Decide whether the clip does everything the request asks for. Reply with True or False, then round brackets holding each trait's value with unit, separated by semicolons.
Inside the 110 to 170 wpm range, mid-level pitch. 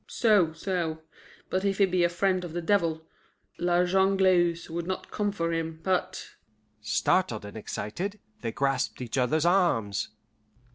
True (155 wpm; 170 Hz)